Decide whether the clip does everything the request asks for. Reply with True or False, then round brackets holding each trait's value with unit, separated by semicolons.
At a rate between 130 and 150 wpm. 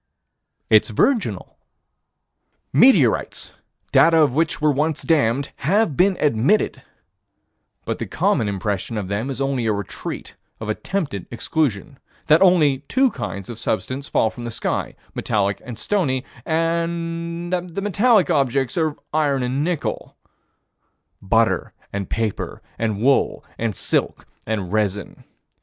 True (135 wpm)